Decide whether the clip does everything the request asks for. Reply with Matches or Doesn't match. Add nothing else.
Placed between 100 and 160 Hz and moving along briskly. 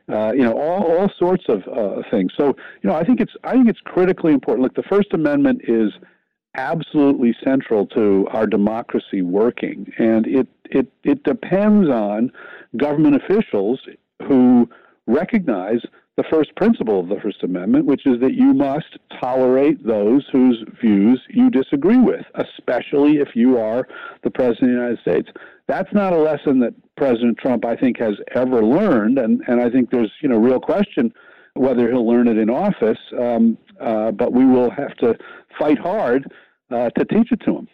Doesn't match